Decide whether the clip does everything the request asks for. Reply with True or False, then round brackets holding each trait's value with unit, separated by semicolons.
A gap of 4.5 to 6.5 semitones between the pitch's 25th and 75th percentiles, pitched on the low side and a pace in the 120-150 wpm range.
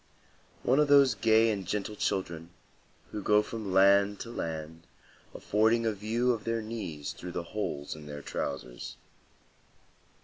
True (5.1 semitones; 105 Hz; 145 wpm)